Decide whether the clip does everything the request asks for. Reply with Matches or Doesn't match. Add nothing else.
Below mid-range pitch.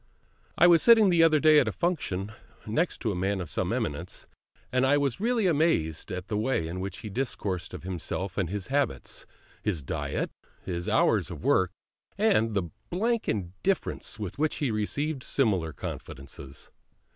Matches